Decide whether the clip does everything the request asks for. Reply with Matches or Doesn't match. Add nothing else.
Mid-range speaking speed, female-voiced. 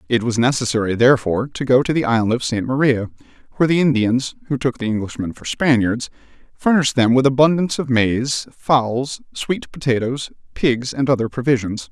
Doesn't match